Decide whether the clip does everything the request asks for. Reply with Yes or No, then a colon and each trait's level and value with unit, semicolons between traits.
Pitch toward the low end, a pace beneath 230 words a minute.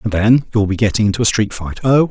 No: low, 110 Hz; fast, 255 wpm